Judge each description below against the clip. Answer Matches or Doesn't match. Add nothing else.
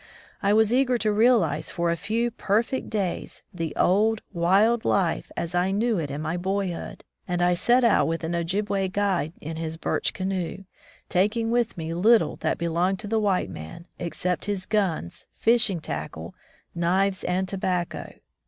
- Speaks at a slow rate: Doesn't match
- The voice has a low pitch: Doesn't match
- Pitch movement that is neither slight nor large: Matches